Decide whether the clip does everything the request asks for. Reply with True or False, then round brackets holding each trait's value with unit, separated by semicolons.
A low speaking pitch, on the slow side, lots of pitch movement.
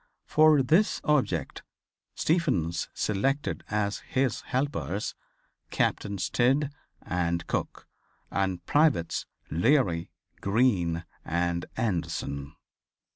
True (100 Hz; 80 wpm; 8.0 semitones)